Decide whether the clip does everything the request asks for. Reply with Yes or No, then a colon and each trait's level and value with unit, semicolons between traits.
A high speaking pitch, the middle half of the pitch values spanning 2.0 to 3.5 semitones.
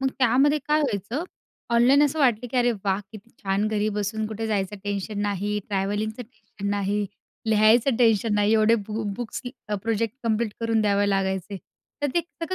Yes: high, 215 Hz; average, 2.9 semitones